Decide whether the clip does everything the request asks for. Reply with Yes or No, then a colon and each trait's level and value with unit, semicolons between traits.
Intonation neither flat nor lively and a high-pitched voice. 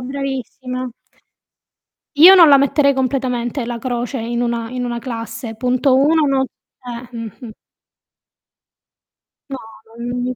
No: narrow, 2.3 semitones; very high, 250 Hz